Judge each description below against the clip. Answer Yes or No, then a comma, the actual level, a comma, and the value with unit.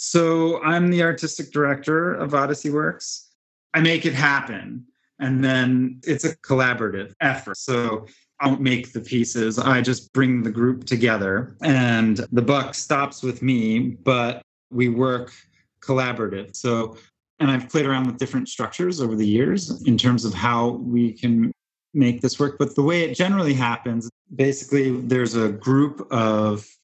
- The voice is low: Yes, low, 130 Hz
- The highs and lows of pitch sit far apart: No, average, 3.0 semitones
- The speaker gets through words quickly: No, average, 160 wpm